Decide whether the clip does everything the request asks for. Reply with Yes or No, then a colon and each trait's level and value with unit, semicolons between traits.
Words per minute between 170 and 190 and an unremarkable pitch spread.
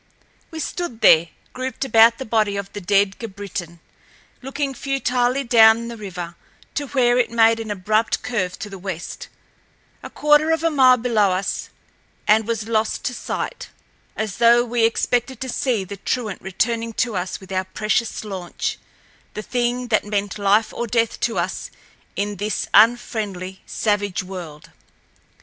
No: average, 155 wpm; average, 3.4 semitones